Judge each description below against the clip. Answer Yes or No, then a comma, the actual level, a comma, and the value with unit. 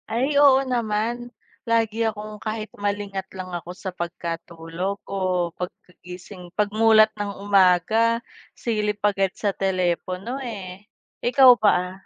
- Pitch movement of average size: Yes, average, 3.0 semitones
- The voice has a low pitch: No, high, 200 Hz